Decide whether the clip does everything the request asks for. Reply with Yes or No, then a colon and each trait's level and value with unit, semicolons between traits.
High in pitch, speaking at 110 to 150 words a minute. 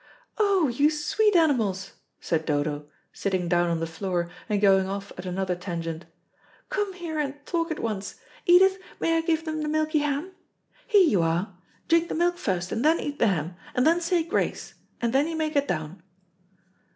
No: very high, 265 Hz; average, 190 wpm